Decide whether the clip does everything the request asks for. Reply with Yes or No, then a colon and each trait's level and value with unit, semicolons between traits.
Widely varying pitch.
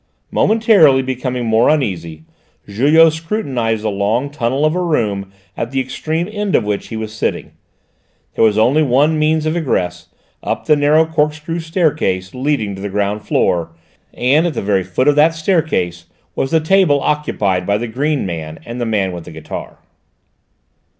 Yes: wide, 7.3 semitones